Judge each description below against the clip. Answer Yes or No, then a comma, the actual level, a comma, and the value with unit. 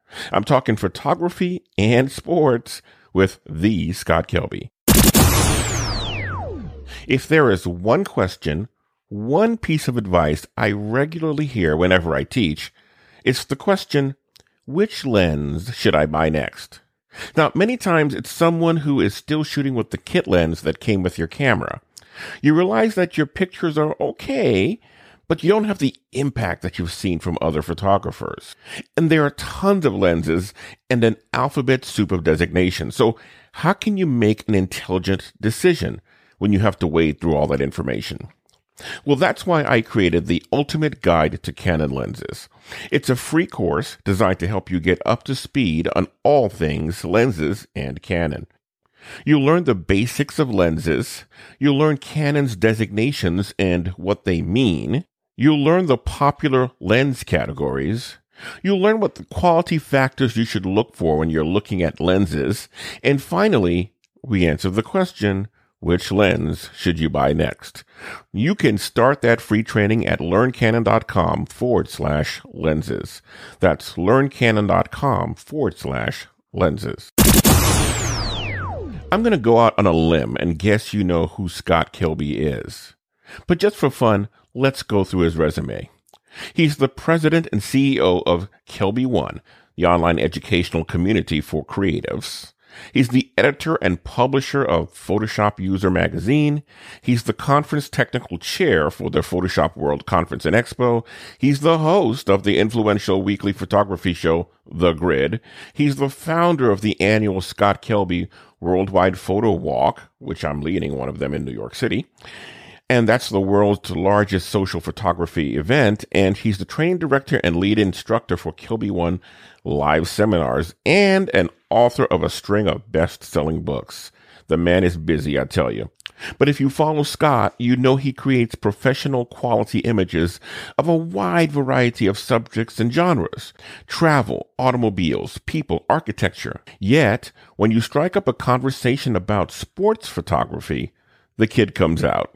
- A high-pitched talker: No, low, 105 Hz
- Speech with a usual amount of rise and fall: No, wide, 7.5 semitones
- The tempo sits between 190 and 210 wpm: No, average, 150 wpm